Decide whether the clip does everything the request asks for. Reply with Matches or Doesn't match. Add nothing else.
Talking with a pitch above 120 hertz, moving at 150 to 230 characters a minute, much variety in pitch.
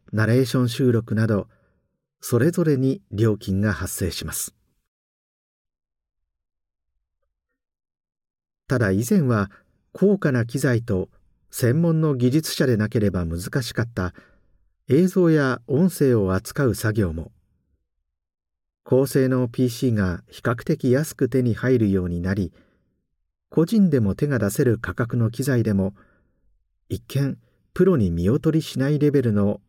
Doesn't match